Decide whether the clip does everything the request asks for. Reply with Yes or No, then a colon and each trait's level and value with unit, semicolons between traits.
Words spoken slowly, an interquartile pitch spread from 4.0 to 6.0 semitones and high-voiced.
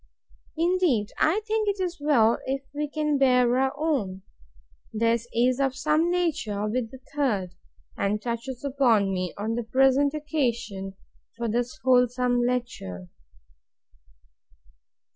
Yes: slow, 130 wpm; average, 4.4 semitones; very high, 250 Hz